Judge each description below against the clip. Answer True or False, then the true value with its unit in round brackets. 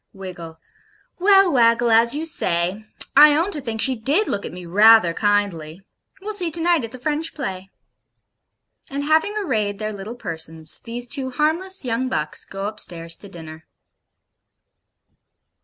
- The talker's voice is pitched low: False (230 Hz)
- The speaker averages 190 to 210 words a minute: False (155 wpm)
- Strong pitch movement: True (8.0 semitones)